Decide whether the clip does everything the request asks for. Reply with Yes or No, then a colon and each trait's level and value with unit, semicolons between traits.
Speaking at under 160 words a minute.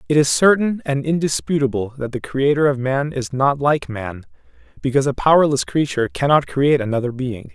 No: average, 175 wpm